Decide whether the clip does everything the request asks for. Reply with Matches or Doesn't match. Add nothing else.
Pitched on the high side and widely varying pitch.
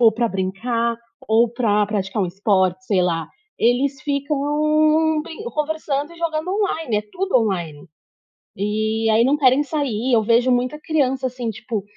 Matches